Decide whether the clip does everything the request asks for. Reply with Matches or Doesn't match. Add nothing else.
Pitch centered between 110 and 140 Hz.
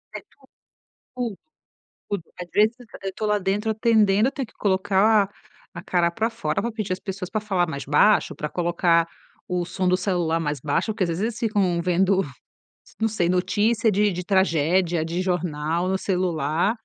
Doesn't match